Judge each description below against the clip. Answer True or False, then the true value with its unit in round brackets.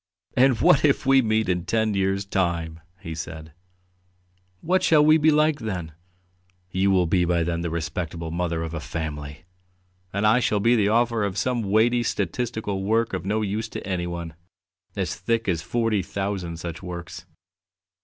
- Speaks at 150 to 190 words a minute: True (170 wpm)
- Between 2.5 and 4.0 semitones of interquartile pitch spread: False (5.1 semitones)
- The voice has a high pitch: False (95 Hz)